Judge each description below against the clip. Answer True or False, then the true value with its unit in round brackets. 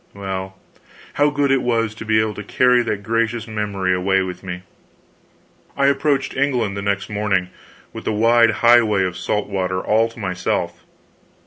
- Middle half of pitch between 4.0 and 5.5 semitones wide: False (3.5 semitones)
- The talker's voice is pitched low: True (105 Hz)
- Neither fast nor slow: True (165 wpm)